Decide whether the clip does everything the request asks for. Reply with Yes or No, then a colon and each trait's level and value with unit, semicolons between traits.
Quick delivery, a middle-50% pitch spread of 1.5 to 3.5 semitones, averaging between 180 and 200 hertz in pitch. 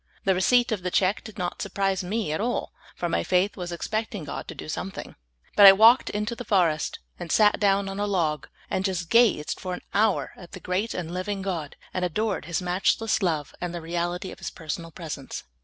Yes: fast, 225 wpm; average, 3.1 semitones; medium, 185 Hz